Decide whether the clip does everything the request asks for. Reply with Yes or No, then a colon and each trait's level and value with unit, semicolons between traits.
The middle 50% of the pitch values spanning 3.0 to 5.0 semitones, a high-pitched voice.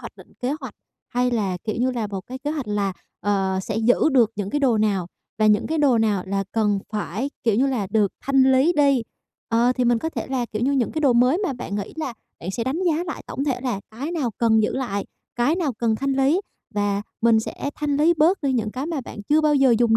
Yes: average, 4.5 semitones; high, 245 Hz